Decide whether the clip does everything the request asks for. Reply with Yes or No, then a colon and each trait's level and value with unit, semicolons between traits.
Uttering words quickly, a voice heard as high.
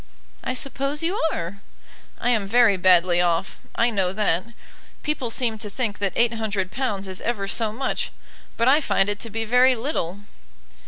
No: average, 165 wpm; high, 220 Hz